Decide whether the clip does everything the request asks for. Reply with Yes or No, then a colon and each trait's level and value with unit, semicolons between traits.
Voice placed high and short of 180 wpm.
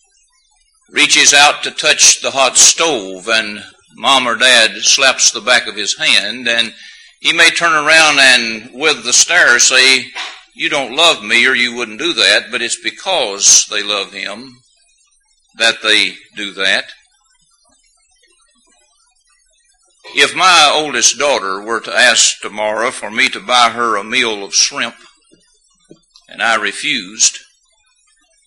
Yes: high, 195 Hz; average, 140 wpm